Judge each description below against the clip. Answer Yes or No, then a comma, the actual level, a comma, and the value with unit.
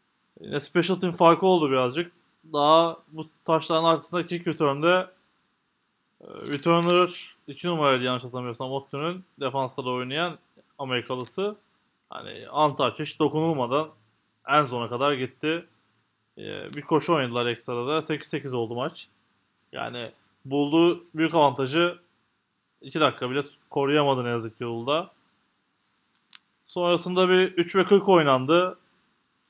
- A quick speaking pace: No, average, 110 wpm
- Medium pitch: Yes, medium, 155 Hz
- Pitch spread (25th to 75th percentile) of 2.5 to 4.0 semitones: No, average, 4.6 semitones